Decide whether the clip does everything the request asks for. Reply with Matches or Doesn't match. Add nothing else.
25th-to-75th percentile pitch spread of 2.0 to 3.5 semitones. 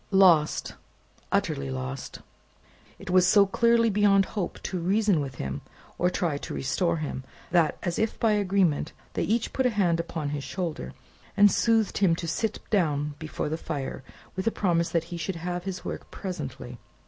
Doesn't match